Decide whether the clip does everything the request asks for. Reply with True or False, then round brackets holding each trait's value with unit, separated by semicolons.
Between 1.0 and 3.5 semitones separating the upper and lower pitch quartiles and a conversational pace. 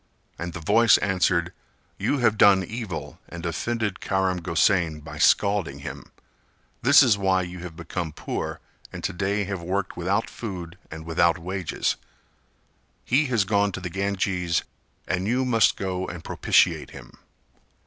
True (3.0 semitones; 150 wpm)